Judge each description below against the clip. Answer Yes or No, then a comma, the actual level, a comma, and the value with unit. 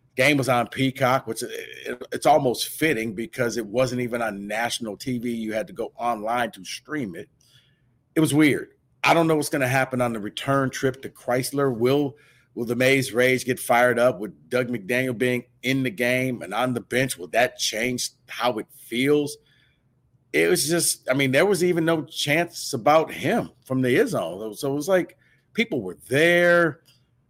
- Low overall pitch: Yes, low, 130 Hz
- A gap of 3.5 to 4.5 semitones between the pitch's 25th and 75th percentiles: No, average, 2.9 semitones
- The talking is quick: No, average, 190 wpm